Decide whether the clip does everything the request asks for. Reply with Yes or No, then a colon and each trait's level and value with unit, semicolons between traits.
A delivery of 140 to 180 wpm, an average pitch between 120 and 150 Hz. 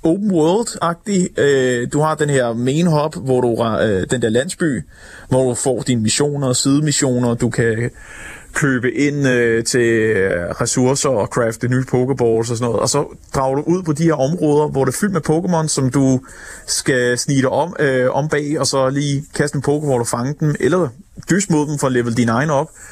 No: average, 195 wpm; low, 135 Hz